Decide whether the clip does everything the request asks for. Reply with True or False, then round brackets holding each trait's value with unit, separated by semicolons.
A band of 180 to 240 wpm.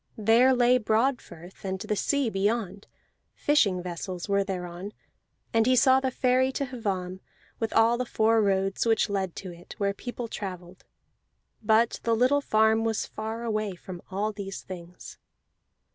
False (155 wpm)